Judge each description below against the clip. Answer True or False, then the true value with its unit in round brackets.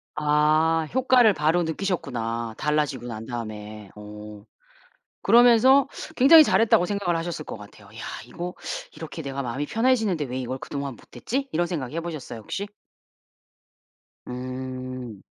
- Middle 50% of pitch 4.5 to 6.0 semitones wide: False (6.7 semitones)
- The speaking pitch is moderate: True (150 Hz)